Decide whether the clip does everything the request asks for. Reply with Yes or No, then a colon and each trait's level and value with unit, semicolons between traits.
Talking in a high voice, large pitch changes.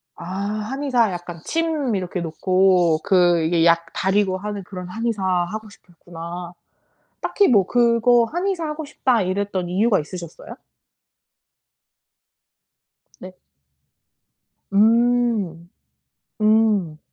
No: high, 195 Hz; average, 4.7 semitones